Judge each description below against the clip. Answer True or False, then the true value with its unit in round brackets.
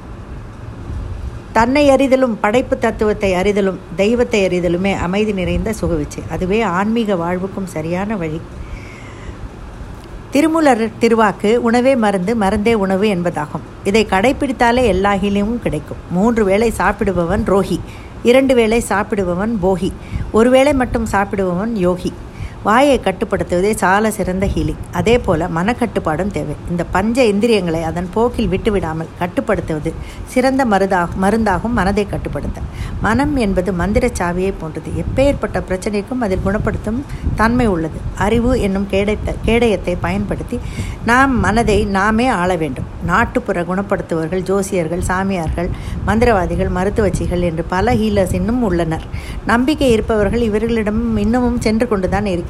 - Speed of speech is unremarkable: True (115 wpm)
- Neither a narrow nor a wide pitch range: True (4.5 semitones)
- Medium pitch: False (200 Hz)